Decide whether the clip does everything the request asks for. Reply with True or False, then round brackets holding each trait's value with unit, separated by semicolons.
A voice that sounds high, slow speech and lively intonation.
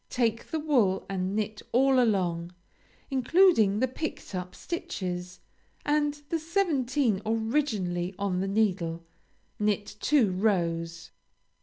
True (215 Hz; 115 wpm; 6.9 semitones)